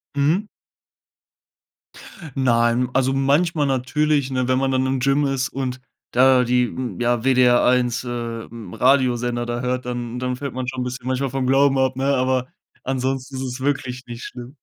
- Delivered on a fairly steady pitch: Yes, narrow, 1.4 semitones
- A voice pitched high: No, low, 130 Hz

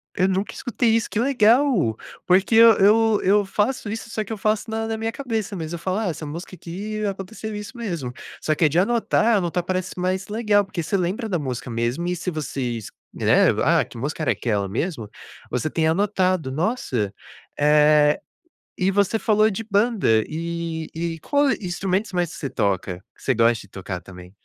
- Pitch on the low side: No, medium, 185 Hz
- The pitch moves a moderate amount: No, wide, 5.9 semitones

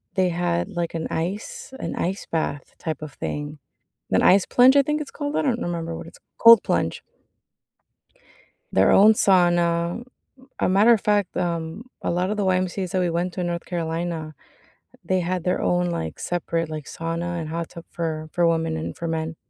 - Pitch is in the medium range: Yes, medium, 175 Hz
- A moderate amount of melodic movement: No, narrow, 2.3 semitones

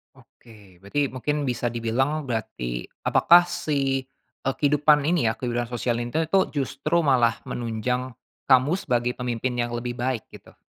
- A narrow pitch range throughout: No, average, 3.2 semitones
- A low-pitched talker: Yes, low, 125 Hz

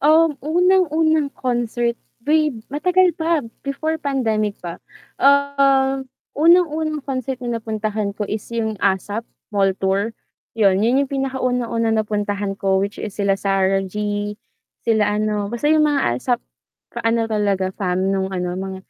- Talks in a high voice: Yes, high, 230 Hz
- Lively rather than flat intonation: Yes, wide, 5.7 semitones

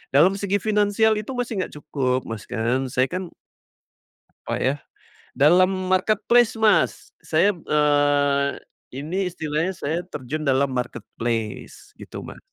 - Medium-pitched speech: Yes, medium, 155 Hz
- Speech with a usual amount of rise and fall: No, wide, 6.1 semitones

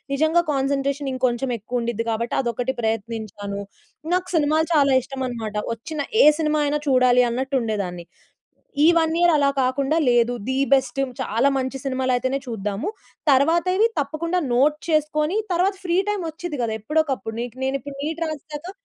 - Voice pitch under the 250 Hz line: No, very high, 270 Hz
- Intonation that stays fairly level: No, average, 4.3 semitones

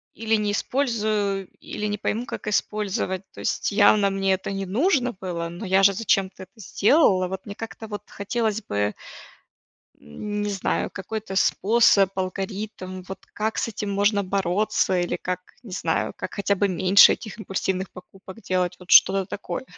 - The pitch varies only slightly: Yes, narrow, 2.1 semitones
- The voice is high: Yes, high, 200 Hz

